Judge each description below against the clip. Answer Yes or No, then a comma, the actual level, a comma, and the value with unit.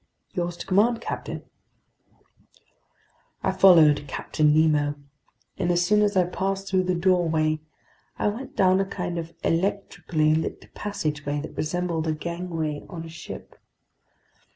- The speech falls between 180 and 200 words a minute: No, slow, 135 wpm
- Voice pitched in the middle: Yes, medium, 175 Hz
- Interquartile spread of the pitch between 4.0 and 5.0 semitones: No, average, 3.4 semitones